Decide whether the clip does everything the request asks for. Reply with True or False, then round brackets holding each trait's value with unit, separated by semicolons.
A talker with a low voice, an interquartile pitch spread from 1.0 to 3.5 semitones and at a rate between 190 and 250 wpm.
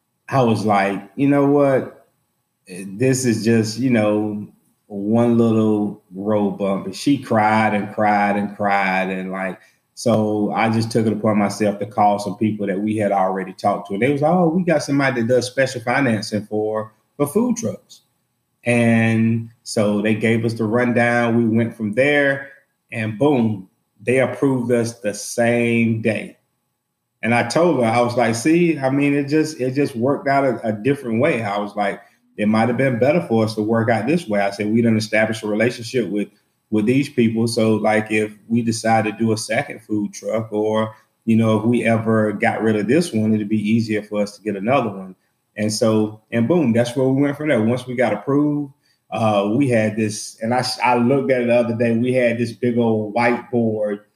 True (115 Hz; 2.6 semitones; 205 wpm)